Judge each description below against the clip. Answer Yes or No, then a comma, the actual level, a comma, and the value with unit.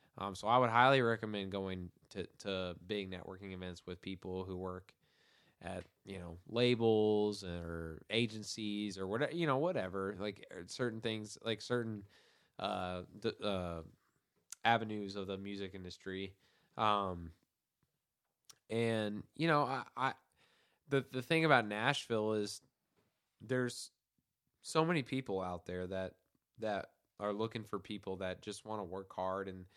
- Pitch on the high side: No, low, 105 Hz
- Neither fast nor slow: Yes, average, 145 wpm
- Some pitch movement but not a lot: Yes, average, 3.6 semitones